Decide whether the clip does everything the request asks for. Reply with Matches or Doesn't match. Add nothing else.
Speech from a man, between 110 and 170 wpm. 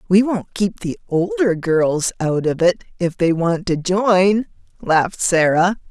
Doesn't match